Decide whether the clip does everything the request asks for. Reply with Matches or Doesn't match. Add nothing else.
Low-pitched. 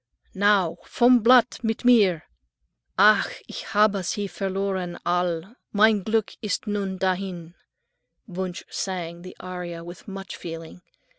Doesn't match